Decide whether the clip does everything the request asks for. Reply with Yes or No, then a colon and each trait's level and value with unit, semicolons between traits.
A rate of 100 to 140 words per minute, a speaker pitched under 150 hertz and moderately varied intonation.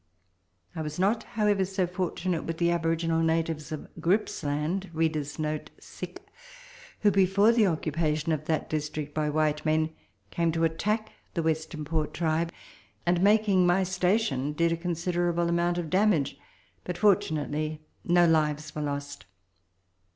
No: slow, 135 wpm; medium, 165 Hz; average, 3.1 semitones